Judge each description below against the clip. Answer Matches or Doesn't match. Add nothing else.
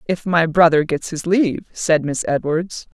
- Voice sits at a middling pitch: Matches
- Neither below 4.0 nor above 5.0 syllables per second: Matches